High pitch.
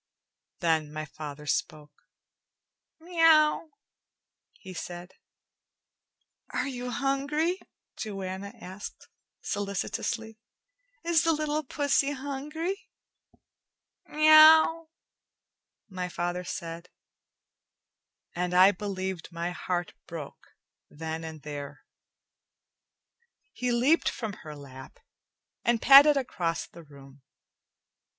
Yes: high, 195 Hz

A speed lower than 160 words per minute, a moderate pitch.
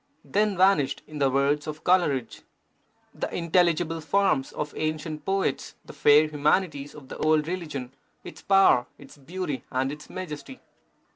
Yes: average, 145 wpm; medium, 155 Hz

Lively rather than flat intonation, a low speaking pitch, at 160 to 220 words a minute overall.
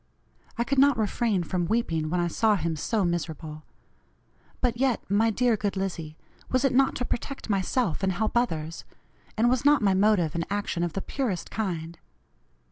No: wide, 5.7 semitones; high, 200 Hz; average, 180 wpm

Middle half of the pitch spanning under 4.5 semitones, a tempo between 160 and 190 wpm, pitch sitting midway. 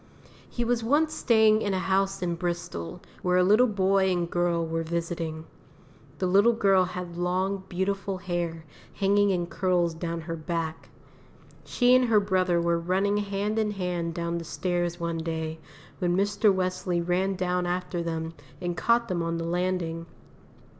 Yes: narrow, 2.6 semitones; average, 165 wpm; medium, 180 Hz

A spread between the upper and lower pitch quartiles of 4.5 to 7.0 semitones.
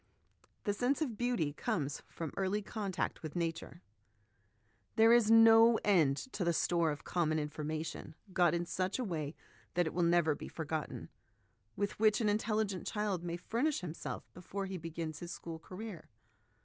Yes: average, 4.8 semitones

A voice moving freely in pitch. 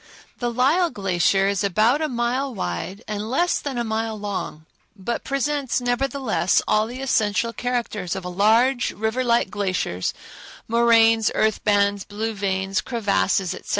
No: average, 3.6 semitones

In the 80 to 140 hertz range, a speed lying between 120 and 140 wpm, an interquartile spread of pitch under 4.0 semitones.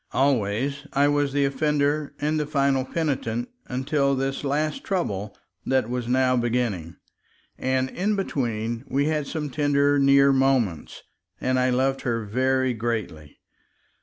Yes: low, 135 Hz; slow, 135 wpm; average, 3.0 semitones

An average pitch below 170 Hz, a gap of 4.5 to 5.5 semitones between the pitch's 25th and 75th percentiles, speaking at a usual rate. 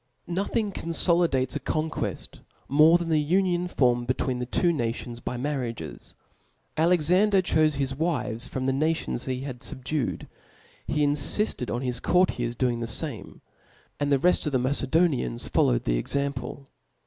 Yes: medium, 140 Hz; average, 5.0 semitones; average, 175 wpm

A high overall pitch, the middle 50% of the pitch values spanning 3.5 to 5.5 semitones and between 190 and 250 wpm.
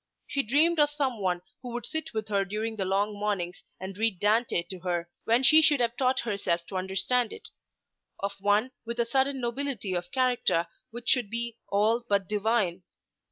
Yes: high, 220 Hz; average, 4.1 semitones; average, 195 wpm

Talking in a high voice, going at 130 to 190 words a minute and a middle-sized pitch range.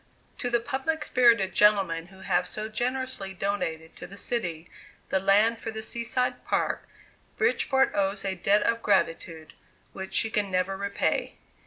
Yes: high, 200 Hz; average, 160 wpm; average, 3.6 semitones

